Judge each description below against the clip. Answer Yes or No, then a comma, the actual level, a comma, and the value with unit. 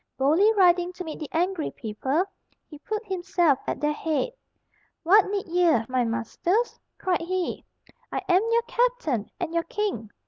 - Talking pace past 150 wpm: Yes, average, 160 wpm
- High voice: Yes, very high, 350 Hz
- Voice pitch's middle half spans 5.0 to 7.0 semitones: No, average, 4.5 semitones